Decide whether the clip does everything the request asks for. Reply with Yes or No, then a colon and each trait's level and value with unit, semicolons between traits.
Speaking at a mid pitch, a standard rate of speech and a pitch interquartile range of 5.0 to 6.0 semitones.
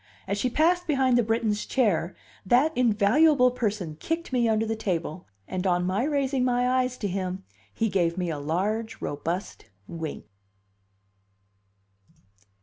No: high, 220 Hz; average, 145 wpm; wide, 5.4 semitones